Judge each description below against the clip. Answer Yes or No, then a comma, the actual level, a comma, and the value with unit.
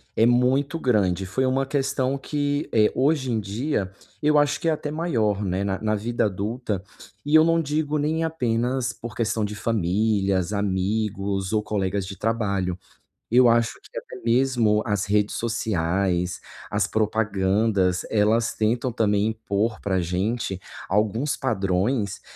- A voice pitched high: No, low, 110 Hz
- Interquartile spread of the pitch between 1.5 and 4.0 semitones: No, average, 4.5 semitones